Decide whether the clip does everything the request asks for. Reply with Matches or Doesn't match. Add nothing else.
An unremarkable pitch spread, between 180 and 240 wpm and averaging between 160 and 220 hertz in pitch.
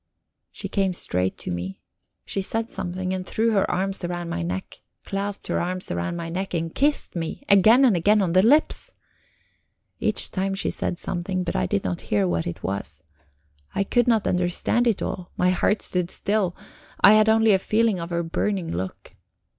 Matches